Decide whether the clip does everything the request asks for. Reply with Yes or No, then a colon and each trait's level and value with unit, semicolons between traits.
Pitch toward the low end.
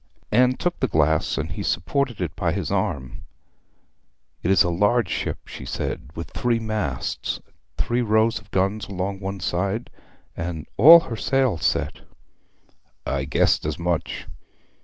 Yes: low, 100 Hz